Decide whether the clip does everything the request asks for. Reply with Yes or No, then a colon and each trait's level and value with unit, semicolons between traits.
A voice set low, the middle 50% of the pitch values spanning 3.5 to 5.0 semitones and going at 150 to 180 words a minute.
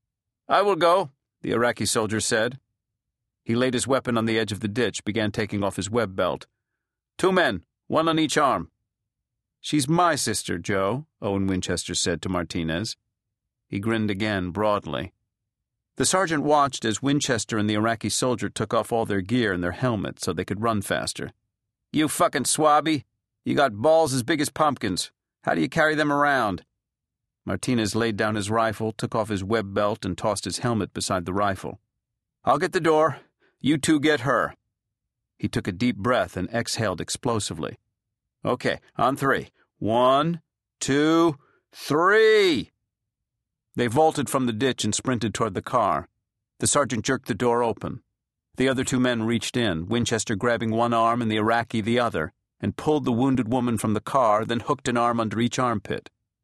Yes: low, 115 Hz; average, 4.0 semitones; average, 175 wpm